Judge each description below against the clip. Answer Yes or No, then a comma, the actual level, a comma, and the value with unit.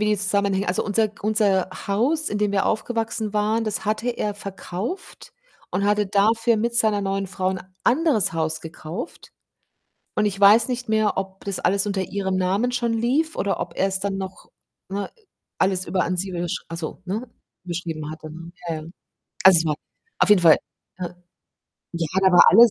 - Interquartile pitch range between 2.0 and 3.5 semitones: Yes, average, 2.9 semitones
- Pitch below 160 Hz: No, high, 200 Hz